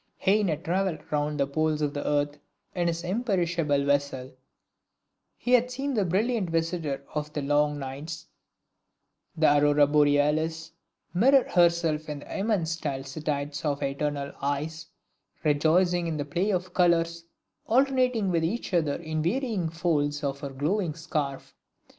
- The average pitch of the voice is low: No, medium, 160 Hz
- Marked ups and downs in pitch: No, average, 3.5 semitones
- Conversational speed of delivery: Yes, average, 145 wpm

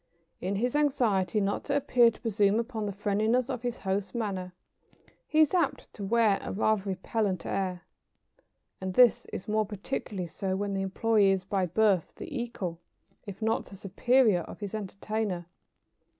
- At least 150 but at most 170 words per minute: Yes, average, 165 wpm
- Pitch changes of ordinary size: Yes, average, 3.3 semitones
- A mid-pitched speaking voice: No, high, 205 Hz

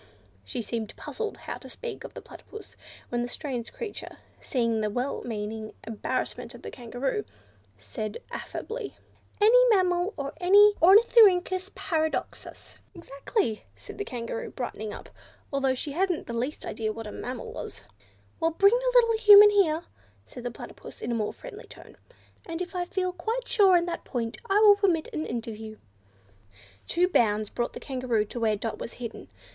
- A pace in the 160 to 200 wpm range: Yes, average, 165 wpm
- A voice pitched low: No, very high, 310 Hz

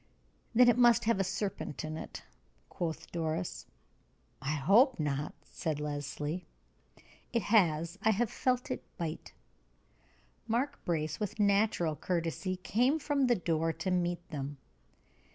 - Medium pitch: Yes, medium, 180 Hz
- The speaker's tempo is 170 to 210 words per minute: No, slow, 135 wpm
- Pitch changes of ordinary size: No, wide, 6.2 semitones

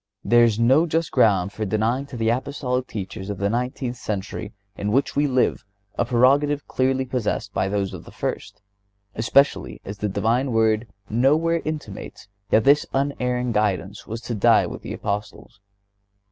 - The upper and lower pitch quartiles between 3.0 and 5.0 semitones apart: Yes, average, 4.2 semitones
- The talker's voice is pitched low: Yes, low, 120 Hz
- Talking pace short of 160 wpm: No, average, 165 wpm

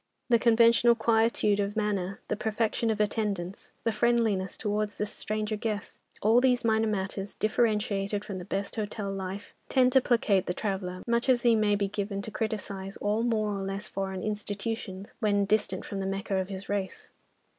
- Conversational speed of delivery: Yes, average, 175 wpm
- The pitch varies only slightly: Yes, narrow, 2.2 semitones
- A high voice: Yes, high, 210 Hz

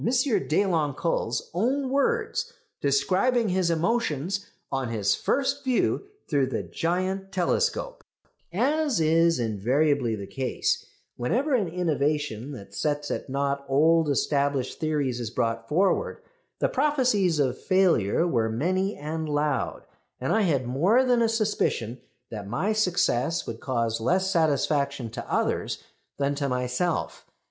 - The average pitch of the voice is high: No, medium, 155 Hz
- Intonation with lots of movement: Yes, wide, 6.7 semitones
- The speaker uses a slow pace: Yes, slow, 130 wpm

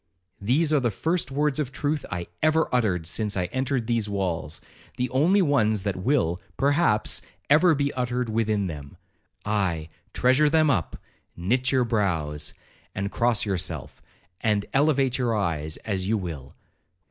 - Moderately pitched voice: No, low, 115 Hz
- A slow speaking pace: No, average, 145 wpm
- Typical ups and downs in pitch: No, wide, 6.7 semitones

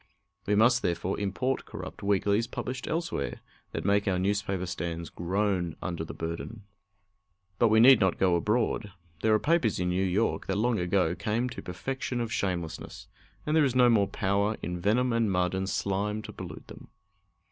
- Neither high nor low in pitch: No, low, 100 Hz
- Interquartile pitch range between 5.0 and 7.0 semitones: No, average, 4.1 semitones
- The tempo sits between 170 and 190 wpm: Yes, average, 180 wpm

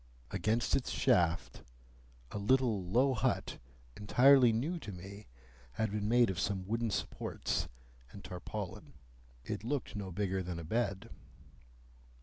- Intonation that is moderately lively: Yes, average, 4.1 semitones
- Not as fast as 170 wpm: Yes, slow, 135 wpm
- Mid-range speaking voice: No, low, 105 Hz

